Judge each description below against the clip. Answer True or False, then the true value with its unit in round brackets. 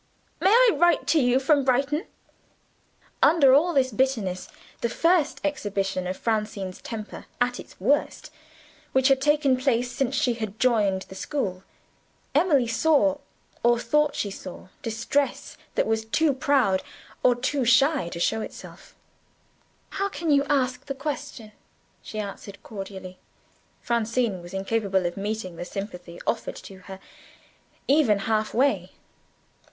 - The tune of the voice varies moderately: False (5.9 semitones)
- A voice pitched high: True (245 Hz)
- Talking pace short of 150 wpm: True (135 wpm)